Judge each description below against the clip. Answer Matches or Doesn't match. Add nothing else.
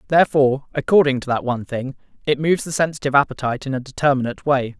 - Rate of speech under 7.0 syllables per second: Doesn't match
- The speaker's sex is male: Matches